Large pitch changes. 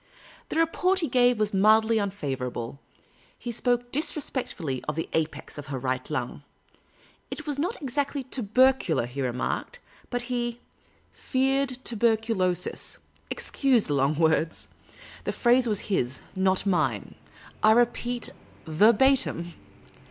Yes: wide, 8.1 semitones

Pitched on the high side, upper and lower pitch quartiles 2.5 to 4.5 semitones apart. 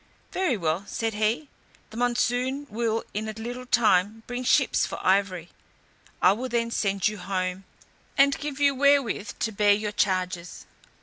Yes: high, 220 Hz; average, 4.0 semitones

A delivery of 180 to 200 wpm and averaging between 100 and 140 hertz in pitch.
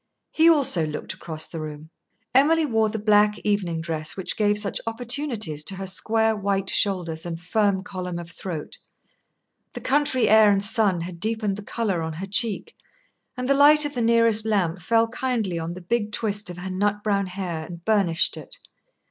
No: average, 185 wpm; high, 205 Hz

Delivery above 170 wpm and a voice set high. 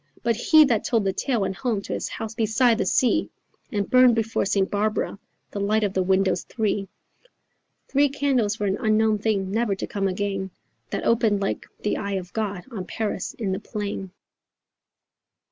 Yes: average, 180 wpm; high, 210 Hz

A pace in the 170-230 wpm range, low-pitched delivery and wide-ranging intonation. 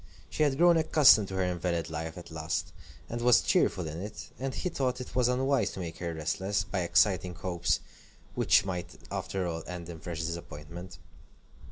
Yes: average, 180 wpm; very low, 90 Hz; wide, 6.0 semitones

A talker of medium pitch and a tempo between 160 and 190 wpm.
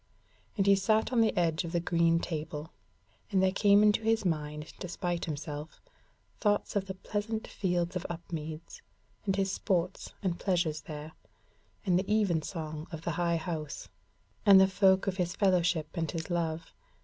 Yes: medium, 175 Hz; average, 170 wpm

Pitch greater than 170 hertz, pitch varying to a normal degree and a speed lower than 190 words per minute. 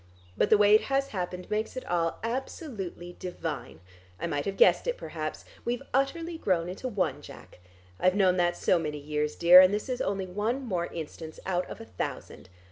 No: high, 190 Hz; average, 5.0 semitones; average, 195 wpm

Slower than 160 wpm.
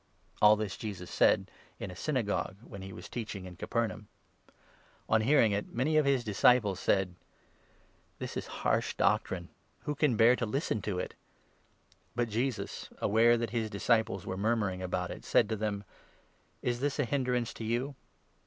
No: average, 175 wpm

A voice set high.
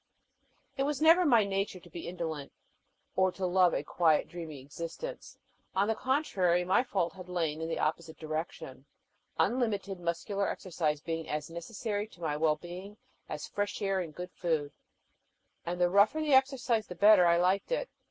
No: medium, 180 Hz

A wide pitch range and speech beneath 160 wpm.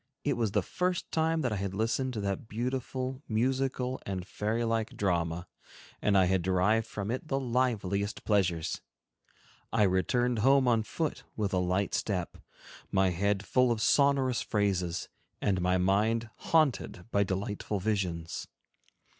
No: average, 4.7 semitones; average, 150 wpm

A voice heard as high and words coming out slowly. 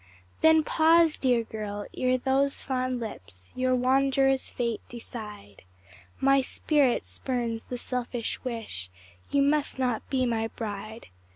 Yes: very high, 250 Hz; slow, 125 wpm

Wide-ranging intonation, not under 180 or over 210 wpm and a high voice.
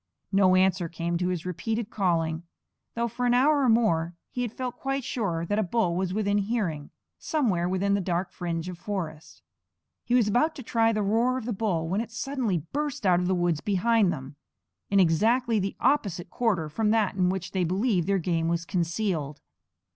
No: average, 4.8 semitones; average, 200 wpm; high, 195 Hz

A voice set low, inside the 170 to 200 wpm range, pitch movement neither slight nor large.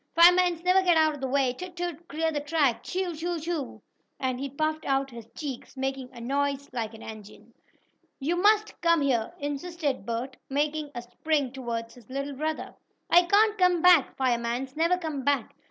No: very high, 285 Hz; average, 185 wpm; average, 4.6 semitones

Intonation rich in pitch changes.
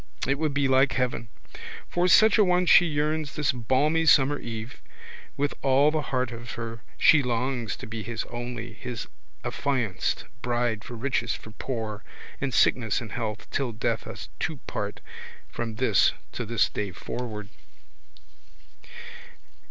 No: average, 3.7 semitones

